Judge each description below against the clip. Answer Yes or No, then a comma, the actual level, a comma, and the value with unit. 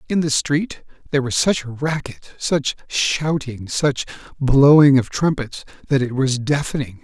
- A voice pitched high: No, medium, 140 Hz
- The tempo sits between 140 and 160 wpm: Yes, average, 155 wpm